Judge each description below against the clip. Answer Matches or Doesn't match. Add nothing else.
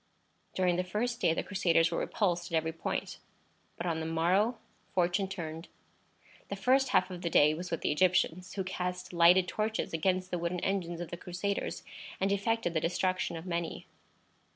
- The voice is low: Doesn't match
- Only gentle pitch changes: Matches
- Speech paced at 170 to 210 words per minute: Matches